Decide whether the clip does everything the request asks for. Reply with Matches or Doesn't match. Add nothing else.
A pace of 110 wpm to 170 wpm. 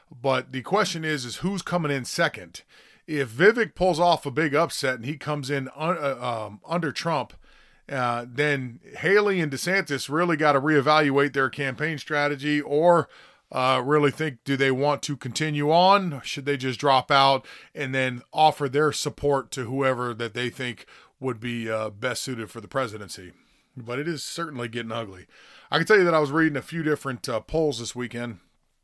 Doesn't match